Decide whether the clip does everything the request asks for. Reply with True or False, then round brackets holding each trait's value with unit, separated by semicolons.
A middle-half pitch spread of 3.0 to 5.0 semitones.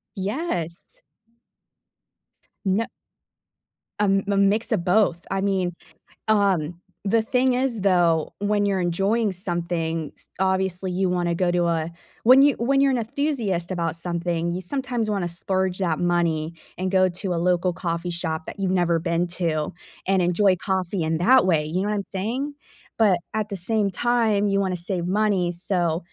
True (3.3 semitones)